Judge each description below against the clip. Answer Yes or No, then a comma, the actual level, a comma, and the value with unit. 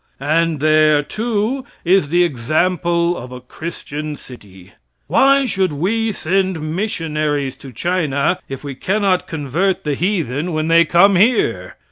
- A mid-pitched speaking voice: Yes, medium, 165 Hz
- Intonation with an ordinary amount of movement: Yes, average, 4.6 semitones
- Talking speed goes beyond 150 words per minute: No, slow, 135 wpm